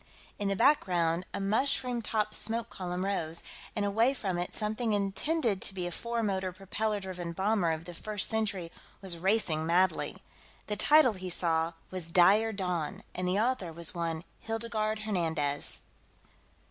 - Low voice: No, high, 195 Hz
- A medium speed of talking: Yes, average, 160 wpm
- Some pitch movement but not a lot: Yes, average, 3.8 semitones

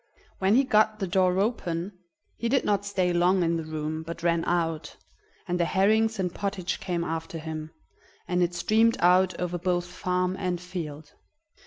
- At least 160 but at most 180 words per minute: Yes, average, 175 wpm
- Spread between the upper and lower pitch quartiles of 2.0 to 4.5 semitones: Yes, narrow, 2.5 semitones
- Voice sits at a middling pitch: Yes, medium, 180 Hz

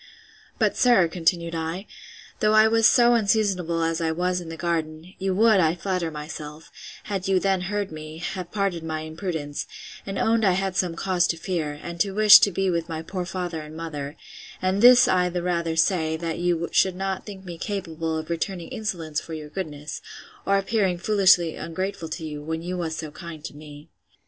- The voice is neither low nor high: Yes, medium, 175 Hz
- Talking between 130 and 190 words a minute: No, average, 200 wpm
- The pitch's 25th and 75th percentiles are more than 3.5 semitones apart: No, average, 3.1 semitones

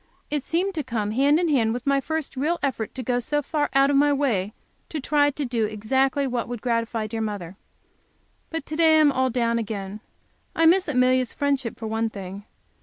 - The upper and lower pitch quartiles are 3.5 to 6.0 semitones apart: Yes, average, 4.5 semitones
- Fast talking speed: Yes, fast, 210 wpm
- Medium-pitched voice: No, very high, 260 Hz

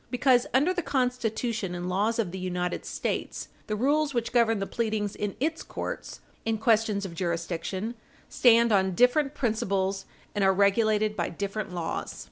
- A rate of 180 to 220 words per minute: No, average, 160 wpm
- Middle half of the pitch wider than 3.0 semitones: Yes, average, 3.9 semitones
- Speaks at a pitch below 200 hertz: No, high, 215 Hz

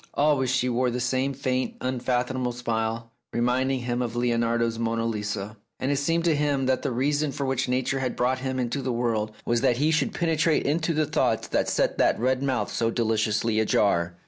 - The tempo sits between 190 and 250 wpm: Yes, average, 200 wpm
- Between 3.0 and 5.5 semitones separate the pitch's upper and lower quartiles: No, narrow, 2.6 semitones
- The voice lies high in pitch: No, low, 125 Hz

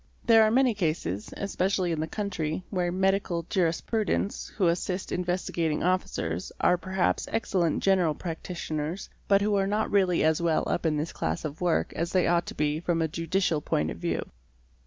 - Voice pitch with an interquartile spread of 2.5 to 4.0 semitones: Yes, average, 3.3 semitones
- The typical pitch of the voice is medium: Yes, medium, 175 Hz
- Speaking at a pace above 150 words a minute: Yes, average, 180 wpm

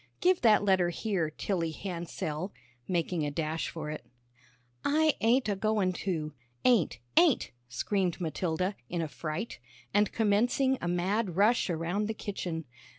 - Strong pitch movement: No, average, 4.6 semitones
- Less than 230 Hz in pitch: Yes, medium, 185 Hz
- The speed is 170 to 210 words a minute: No, average, 145 wpm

